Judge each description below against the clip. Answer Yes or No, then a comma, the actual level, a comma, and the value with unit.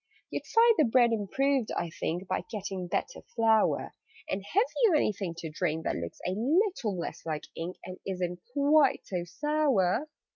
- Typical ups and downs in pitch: No, wide, 8.0 semitones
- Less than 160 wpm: No, average, 170 wpm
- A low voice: No, high, 210 Hz